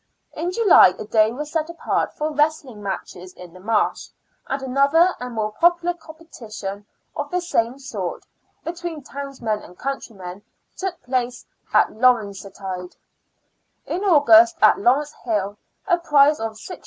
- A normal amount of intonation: No, wide, 7.4 semitones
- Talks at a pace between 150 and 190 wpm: No, average, 140 wpm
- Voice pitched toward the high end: Yes, very high, 265 Hz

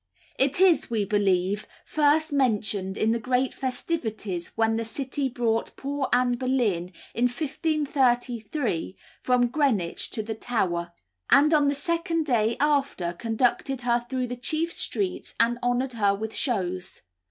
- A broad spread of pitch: No, average, 4.5 semitones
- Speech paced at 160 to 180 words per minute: No, average, 140 wpm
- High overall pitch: Yes, high, 245 Hz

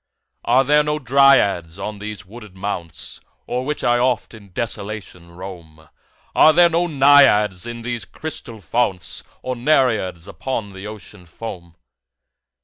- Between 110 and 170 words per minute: Yes, average, 140 wpm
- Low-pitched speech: Yes, low, 110 Hz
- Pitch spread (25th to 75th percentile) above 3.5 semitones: Yes, wide, 5.6 semitones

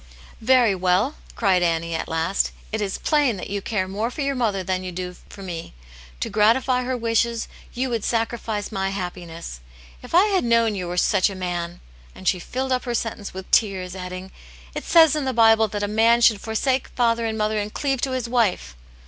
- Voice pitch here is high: Yes, high, 215 Hz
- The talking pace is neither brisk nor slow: No, fast, 210 wpm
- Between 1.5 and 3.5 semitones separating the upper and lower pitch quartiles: No, average, 4.4 semitones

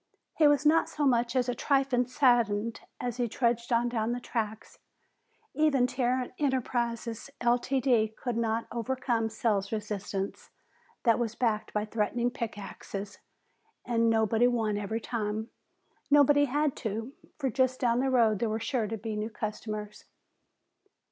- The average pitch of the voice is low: No, high, 235 Hz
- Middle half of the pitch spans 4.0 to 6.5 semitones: No, narrow, 2.6 semitones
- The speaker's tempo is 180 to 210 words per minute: No, average, 150 wpm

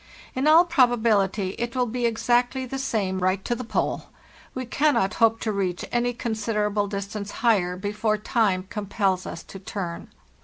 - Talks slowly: No, average, 165 wpm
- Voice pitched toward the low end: No, high, 215 Hz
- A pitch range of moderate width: Yes, average, 3.7 semitones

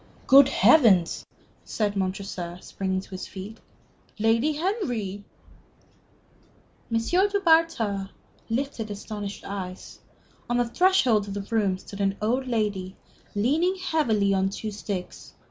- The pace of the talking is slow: Yes, slow, 120 wpm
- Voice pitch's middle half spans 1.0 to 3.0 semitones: No, average, 5.2 semitones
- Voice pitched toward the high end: Yes, high, 215 Hz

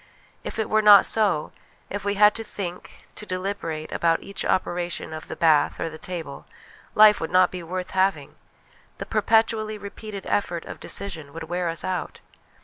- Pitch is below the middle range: No, medium, 185 Hz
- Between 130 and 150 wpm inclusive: No, average, 175 wpm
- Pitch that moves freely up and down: No, average, 3.7 semitones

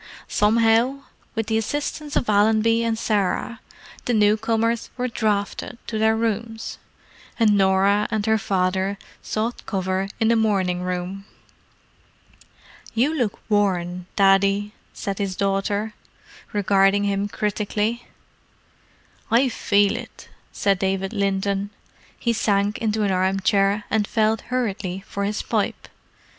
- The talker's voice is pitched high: Yes, high, 205 Hz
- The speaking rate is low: Yes, slow, 120 wpm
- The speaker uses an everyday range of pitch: No, narrow, 2.2 semitones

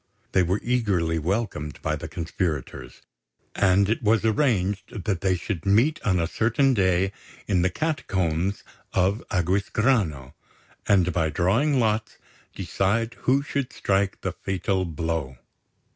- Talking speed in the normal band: No, slow, 130 wpm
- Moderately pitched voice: No, very low, 95 Hz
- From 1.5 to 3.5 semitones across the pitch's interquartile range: No, average, 4.3 semitones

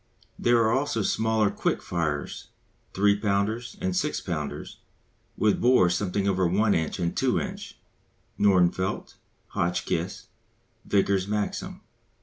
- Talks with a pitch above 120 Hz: No, low, 100 Hz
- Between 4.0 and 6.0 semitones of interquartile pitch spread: No, average, 3.6 semitones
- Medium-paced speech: No, slow, 120 wpm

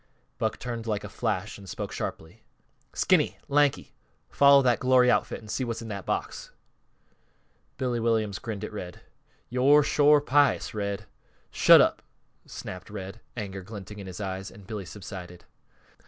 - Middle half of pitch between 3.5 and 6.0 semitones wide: Yes, average, 4.2 semitones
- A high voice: No, low, 110 Hz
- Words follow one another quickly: No, average, 155 wpm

